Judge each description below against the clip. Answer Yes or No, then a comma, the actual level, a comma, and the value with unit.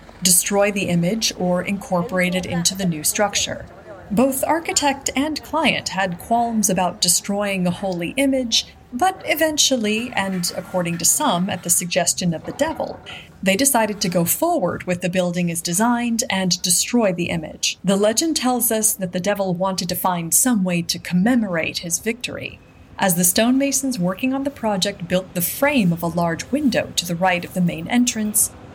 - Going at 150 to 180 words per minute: Yes, average, 175 wpm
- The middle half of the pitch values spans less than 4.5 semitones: No, average, 5.3 semitones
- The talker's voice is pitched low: No, high, 195 Hz